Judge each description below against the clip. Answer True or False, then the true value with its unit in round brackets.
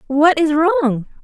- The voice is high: True (305 Hz)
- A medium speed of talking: True (145 wpm)